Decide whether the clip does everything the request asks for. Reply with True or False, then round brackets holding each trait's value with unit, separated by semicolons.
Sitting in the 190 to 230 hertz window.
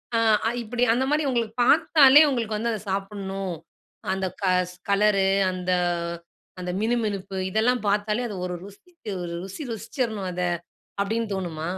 True (210 Hz)